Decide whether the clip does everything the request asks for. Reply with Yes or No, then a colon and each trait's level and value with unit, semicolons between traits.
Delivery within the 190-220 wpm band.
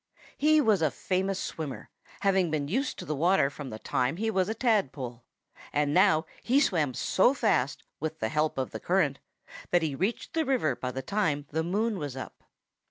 Yes: average, 195 wpm